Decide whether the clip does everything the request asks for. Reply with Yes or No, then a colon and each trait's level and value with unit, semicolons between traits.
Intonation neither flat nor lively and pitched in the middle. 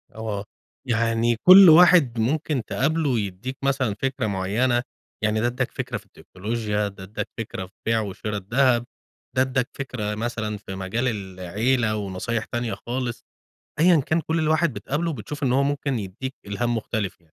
No: average, 4.2 semitones; low, 120 Hz